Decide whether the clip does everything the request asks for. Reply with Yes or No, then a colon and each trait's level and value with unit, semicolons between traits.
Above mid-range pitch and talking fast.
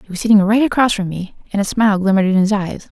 Yes: high, 205 Hz; fast, 280 wpm